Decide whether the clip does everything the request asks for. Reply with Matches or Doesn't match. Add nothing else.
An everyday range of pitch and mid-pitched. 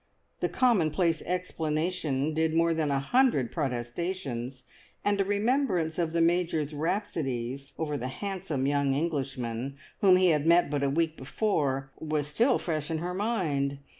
Matches